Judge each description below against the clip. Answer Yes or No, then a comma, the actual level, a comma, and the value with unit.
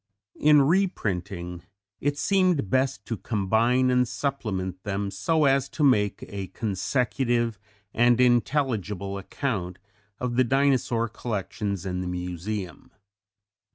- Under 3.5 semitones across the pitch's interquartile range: No, average, 5.2 semitones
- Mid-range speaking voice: No, low, 115 Hz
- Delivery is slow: Yes, slow, 115 wpm